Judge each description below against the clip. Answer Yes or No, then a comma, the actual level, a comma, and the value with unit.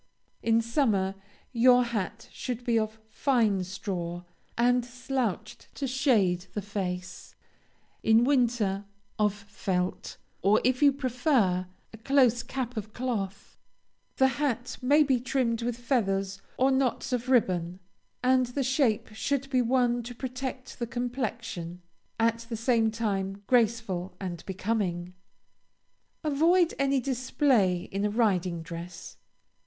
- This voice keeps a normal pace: No, slow, 125 wpm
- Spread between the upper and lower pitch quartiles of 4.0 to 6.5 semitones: Yes, average, 4.5 semitones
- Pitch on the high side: Yes, high, 230 Hz